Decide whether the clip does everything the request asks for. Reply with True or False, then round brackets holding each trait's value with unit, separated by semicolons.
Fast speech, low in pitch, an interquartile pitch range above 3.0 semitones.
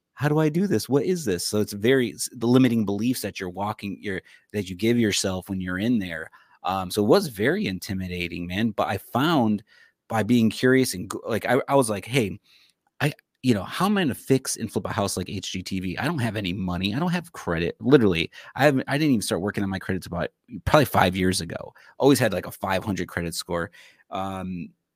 True (225 wpm; 105 Hz; 4.3 semitones)